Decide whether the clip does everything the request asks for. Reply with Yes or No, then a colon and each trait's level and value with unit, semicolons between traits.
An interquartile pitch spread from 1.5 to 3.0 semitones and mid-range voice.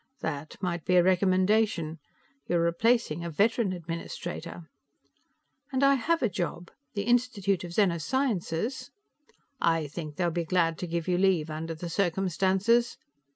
No: average, 4.1 semitones; medium, 180 Hz